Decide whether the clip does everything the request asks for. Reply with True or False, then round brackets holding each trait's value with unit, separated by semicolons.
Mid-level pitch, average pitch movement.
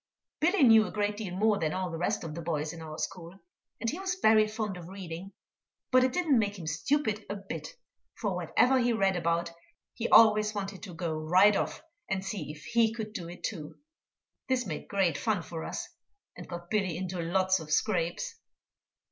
False (195 Hz; 4.4 semitones)